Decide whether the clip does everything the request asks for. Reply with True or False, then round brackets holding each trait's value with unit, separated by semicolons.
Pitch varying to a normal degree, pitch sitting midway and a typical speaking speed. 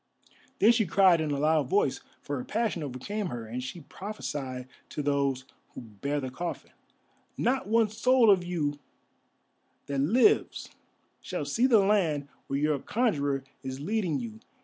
False (7.2 semitones; 155 Hz; 155 wpm)